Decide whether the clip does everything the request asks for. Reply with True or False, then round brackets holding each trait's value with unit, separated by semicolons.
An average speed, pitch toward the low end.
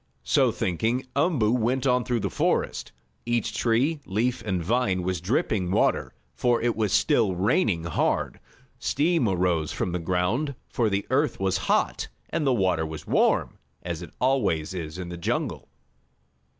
True (160 wpm; 105 Hz)